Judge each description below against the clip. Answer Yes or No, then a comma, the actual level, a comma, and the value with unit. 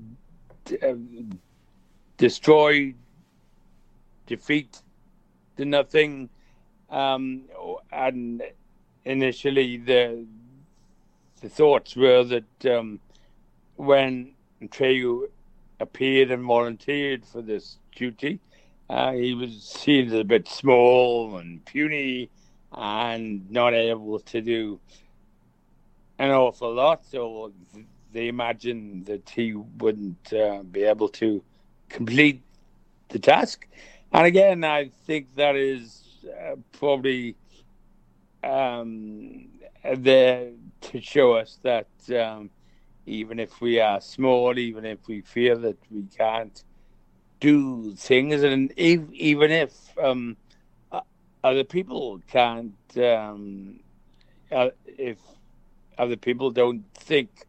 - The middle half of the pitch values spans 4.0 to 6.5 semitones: No, average, 3.4 semitones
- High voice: No, low, 120 Hz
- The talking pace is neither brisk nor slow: No, slow, 100 wpm